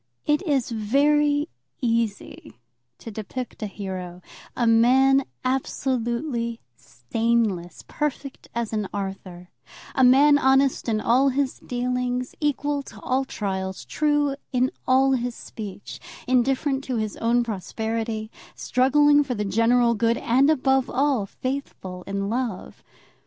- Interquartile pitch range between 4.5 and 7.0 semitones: No, average, 3.8 semitones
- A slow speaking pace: Yes, slow, 125 wpm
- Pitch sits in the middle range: No, high, 245 Hz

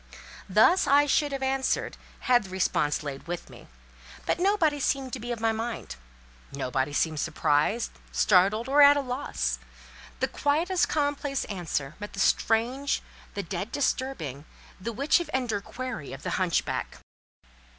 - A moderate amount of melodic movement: No, wide, 7.9 semitones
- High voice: Yes, high, 235 Hz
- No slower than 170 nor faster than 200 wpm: No, average, 150 wpm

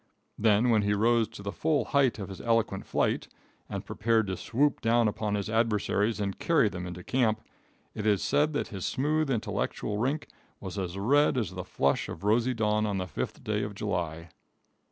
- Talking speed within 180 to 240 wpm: Yes, average, 195 wpm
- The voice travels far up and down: No, average, 3.0 semitones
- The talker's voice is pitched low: Yes, low, 105 Hz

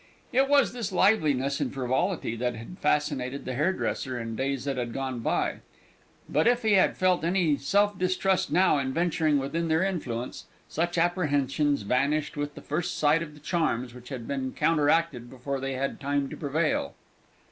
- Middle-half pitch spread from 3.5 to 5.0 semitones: Yes, average, 4.7 semitones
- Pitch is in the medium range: Yes, medium, 145 Hz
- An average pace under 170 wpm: No, average, 175 wpm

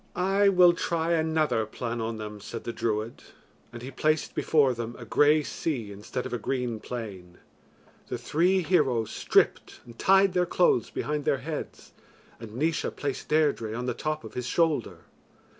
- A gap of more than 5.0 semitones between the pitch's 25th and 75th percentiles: Yes, wide, 5.6 semitones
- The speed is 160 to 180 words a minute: Yes, average, 170 wpm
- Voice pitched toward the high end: No, low, 130 Hz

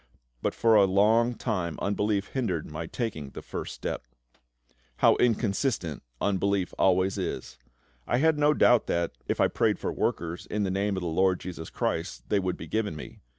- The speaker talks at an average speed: Yes, average, 180 wpm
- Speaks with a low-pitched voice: Yes, low, 100 Hz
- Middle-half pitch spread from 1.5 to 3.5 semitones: No, average, 4.3 semitones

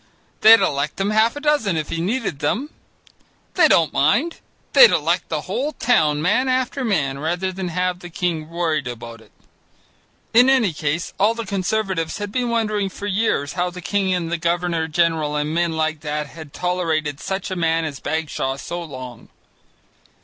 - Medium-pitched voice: Yes, medium, 175 Hz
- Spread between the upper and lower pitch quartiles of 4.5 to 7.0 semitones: Yes, average, 4.9 semitones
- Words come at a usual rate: Yes, average, 180 wpm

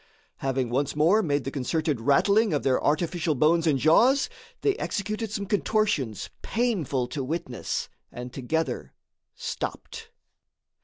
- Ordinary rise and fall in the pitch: No, wide, 7.3 semitones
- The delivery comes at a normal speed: No, slow, 125 wpm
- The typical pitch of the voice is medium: Yes, medium, 155 Hz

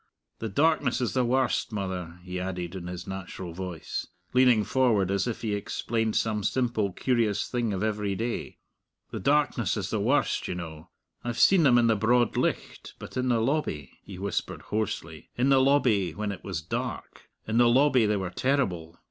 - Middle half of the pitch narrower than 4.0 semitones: No, average, 4.7 semitones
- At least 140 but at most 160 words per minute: No, average, 185 wpm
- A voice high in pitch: No, low, 110 Hz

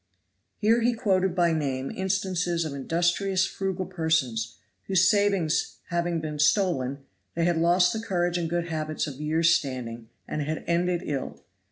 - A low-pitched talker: No, medium, 170 Hz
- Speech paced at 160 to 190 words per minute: No, average, 150 wpm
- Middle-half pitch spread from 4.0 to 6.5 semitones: No, average, 3.5 semitones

